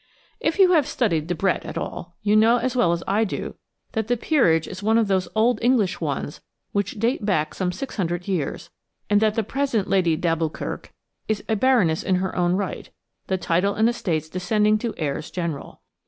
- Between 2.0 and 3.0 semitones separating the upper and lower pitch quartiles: No, average, 4.4 semitones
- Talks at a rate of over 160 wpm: Yes, average, 195 wpm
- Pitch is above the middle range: Yes, high, 200 Hz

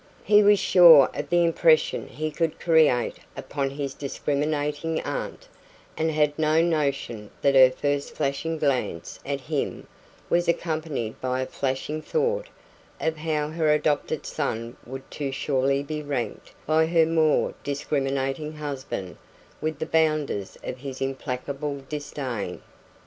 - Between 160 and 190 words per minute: No, slow, 135 wpm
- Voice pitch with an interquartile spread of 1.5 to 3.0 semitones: Yes, average, 2.7 semitones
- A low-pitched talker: No, medium, 145 Hz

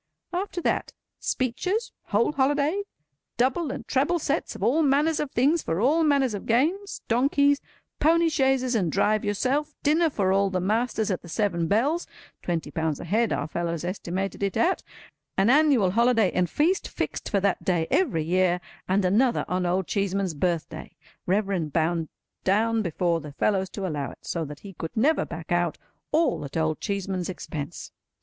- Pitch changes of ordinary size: No, wide, 8.0 semitones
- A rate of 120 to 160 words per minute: No, average, 170 wpm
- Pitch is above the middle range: Yes, high, 205 Hz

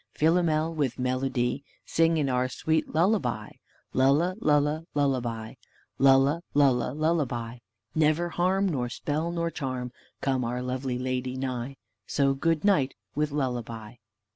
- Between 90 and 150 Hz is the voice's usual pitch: Yes, low, 135 Hz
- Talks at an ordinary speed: No, slow, 125 wpm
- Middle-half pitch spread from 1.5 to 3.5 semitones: No, average, 3.9 semitones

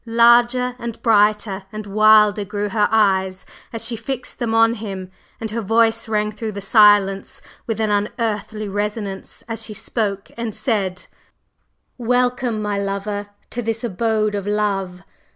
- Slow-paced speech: No, average, 150 wpm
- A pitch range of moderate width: No, narrow, 2.0 semitones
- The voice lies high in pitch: Yes, high, 215 Hz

